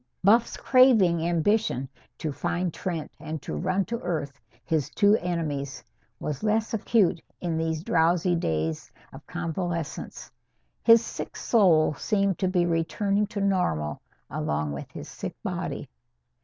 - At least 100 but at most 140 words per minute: Yes, slow, 135 wpm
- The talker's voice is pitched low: No, medium, 175 Hz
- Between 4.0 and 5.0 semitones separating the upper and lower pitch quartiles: Yes, average, 4.3 semitones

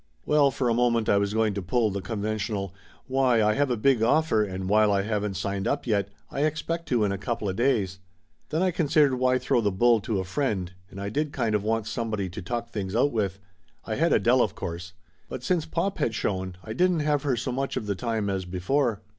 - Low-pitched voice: Yes, low, 110 Hz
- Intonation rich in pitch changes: No, average, 4.8 semitones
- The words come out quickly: Yes, fast, 235 wpm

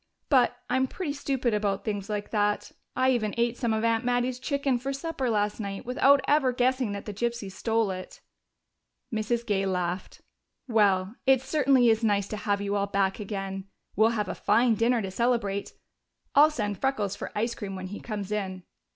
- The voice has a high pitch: Yes, high, 220 Hz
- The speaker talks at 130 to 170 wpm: No, average, 190 wpm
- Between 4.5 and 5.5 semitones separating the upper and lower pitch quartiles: No, average, 3.7 semitones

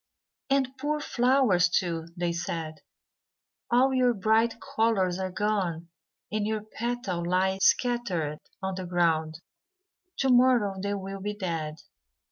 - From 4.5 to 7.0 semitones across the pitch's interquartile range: Yes, average, 5.3 semitones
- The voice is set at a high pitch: Yes, high, 195 Hz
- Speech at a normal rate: No, slow, 125 wpm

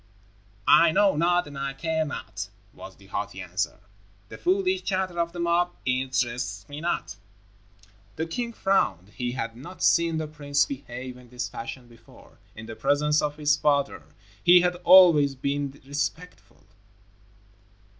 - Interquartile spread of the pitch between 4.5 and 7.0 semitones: Yes, average, 5.0 semitones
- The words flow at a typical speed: Yes, average, 150 wpm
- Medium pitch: Yes, medium, 150 Hz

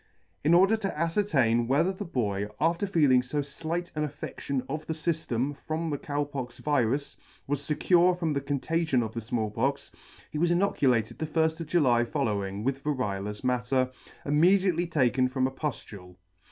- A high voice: No, medium, 145 Hz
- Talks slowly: No, average, 165 wpm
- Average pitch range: Yes, average, 4.7 semitones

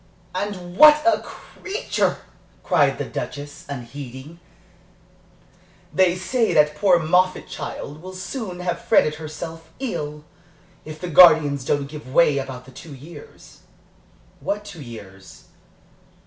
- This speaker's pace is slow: Yes, slow, 120 wpm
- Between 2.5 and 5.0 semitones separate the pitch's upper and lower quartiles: Yes, average, 4.4 semitones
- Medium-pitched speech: Yes, medium, 160 Hz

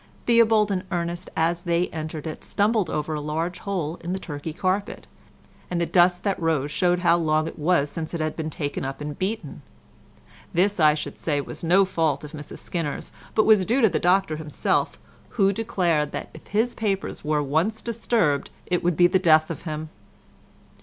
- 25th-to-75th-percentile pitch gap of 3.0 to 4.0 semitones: Yes, average, 3.7 semitones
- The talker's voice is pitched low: No, medium, 170 Hz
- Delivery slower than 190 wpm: No, average, 195 wpm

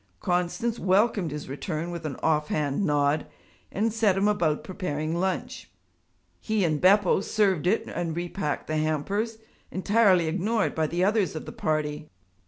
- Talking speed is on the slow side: No, average, 155 wpm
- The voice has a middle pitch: Yes, medium, 175 Hz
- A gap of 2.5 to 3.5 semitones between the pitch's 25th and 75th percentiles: No, average, 4.8 semitones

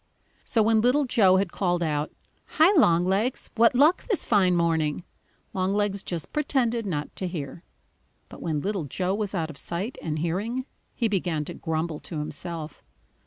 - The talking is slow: No, average, 165 wpm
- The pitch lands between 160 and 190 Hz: Yes, medium, 185 Hz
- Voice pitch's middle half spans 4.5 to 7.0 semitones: Yes, wide, 5.5 semitones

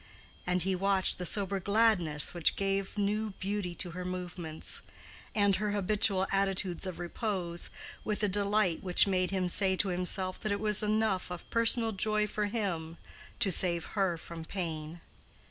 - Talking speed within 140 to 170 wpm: Yes, average, 160 wpm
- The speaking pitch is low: No, high, 190 Hz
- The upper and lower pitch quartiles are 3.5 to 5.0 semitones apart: No, narrow, 2.6 semitones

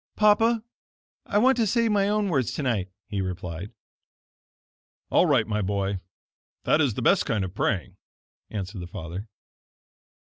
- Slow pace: No, average, 145 wpm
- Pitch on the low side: Yes, low, 110 Hz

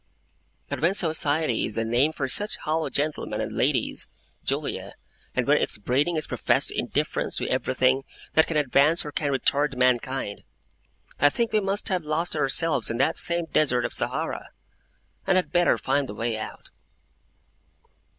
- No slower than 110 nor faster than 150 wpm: No, average, 160 wpm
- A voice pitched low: No, medium, 145 Hz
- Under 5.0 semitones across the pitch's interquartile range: Yes, average, 4.3 semitones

